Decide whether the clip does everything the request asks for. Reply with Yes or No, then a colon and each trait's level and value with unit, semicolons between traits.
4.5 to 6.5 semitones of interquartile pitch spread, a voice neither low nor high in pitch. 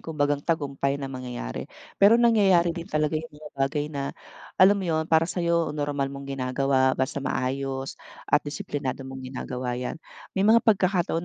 No: average, 3.8 semitones; medium, 145 Hz